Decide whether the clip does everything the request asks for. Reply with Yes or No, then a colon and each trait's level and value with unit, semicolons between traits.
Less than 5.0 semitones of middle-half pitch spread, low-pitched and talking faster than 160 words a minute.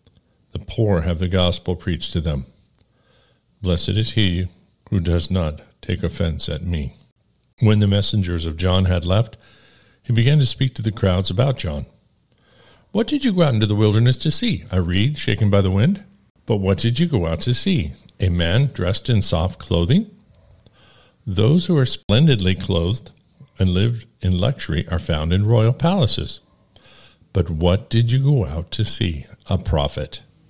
No: wide, 5.5 semitones; low, 100 Hz; average, 175 wpm